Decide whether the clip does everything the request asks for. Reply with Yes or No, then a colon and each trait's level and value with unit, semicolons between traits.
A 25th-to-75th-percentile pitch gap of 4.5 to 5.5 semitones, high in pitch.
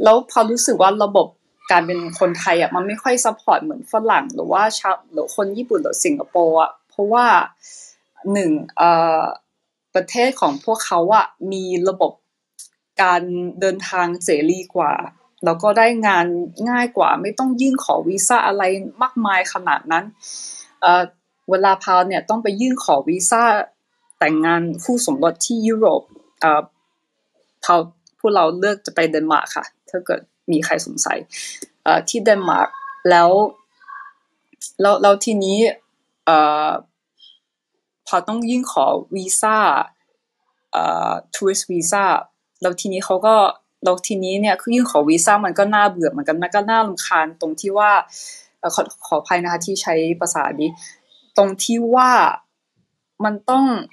Yes: average, 5.1 semitones; high, 200 Hz